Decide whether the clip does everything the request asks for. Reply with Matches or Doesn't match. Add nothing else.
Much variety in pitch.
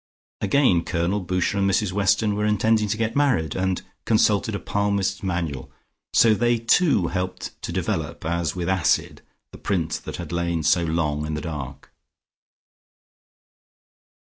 Doesn't match